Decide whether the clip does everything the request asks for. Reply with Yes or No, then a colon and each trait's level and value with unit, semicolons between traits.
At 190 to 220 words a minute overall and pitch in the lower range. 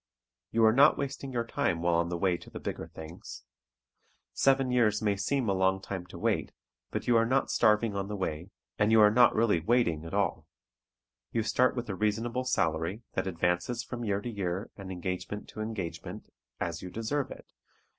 Yes: average, 195 wpm; low, 105 Hz